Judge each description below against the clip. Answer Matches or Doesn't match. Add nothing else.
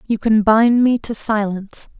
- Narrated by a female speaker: Matches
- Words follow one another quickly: Doesn't match